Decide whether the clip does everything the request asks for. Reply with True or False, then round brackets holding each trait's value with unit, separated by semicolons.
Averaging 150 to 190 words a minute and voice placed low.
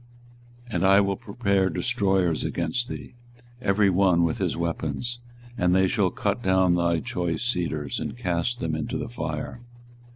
True (160 wpm; 95 Hz)